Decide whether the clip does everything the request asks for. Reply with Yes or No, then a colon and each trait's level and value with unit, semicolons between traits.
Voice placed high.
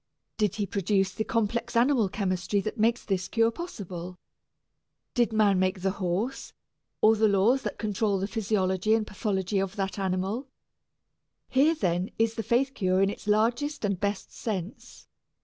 Yes: high, 205 Hz